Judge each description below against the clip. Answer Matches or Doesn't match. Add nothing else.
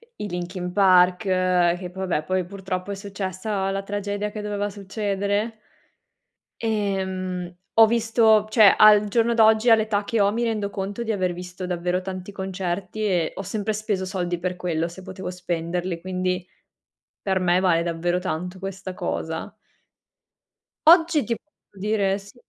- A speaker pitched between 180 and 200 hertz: Matches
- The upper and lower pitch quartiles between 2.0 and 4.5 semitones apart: Matches